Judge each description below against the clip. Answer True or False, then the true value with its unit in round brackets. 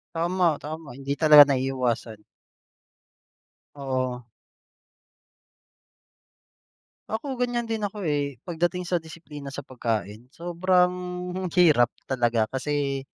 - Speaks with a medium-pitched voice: True (145 Hz)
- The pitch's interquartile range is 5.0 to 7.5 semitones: True (5.3 semitones)